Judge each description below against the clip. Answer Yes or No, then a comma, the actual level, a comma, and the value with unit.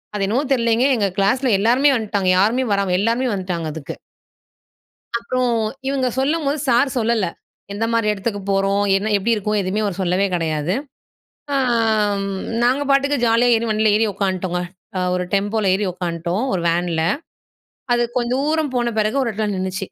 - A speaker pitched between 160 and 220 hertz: Yes, high, 215 Hz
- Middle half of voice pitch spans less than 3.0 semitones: No, average, 3.9 semitones